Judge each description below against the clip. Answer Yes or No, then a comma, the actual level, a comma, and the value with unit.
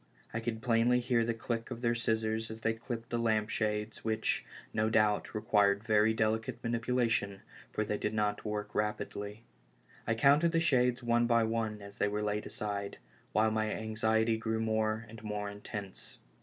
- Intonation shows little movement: Yes, narrow, 1.6 semitones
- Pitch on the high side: No, low, 110 Hz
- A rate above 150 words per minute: Yes, average, 170 wpm